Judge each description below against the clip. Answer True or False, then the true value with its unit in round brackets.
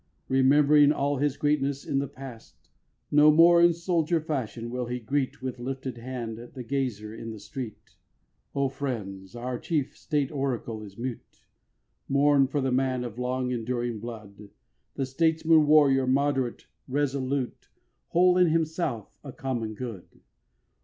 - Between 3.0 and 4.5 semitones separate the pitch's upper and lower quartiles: True (3.4 semitones)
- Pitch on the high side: False (130 Hz)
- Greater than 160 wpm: False (145 wpm)